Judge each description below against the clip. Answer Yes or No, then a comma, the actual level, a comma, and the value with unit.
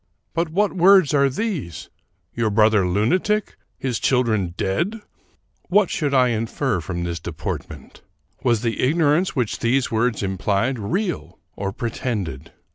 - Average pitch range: No, wide, 7.8 semitones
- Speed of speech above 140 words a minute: No, slow, 135 wpm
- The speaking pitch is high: No, low, 120 Hz